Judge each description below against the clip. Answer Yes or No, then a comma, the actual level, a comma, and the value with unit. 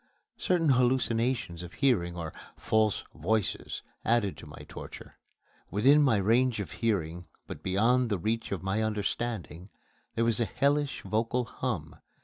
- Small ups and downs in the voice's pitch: No, average, 4.4 semitones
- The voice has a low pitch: Yes, low, 110 Hz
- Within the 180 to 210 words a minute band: No, average, 140 wpm